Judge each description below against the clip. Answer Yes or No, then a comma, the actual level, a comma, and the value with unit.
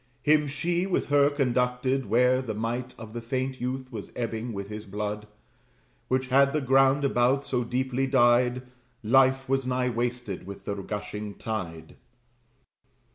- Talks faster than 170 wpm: No, average, 150 wpm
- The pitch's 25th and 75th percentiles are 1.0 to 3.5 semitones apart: Yes, average, 3.1 semitones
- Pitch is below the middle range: Yes, low, 125 Hz